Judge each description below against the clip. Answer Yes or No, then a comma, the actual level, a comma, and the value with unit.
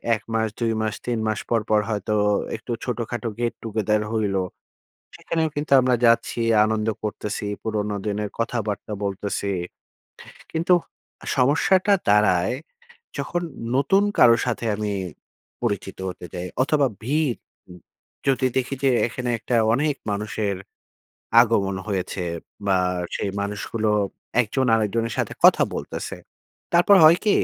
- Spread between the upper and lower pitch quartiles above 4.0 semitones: No, average, 3.6 semitones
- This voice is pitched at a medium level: No, low, 115 Hz